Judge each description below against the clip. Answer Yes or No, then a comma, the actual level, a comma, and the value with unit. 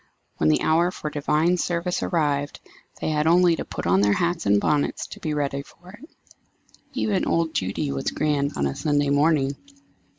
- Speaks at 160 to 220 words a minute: Yes, average, 185 wpm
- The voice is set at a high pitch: No, medium, 150 Hz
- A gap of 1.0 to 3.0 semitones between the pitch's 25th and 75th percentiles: No, average, 3.4 semitones